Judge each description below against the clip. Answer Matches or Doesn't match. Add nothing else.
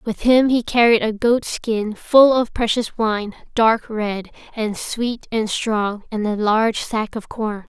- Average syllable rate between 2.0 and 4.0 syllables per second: Matches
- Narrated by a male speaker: Doesn't match